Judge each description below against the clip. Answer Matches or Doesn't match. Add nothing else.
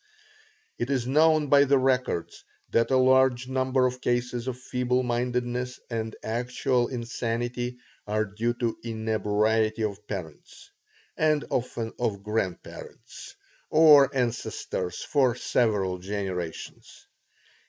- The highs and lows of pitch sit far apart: Doesn't match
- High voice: Doesn't match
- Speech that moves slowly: Matches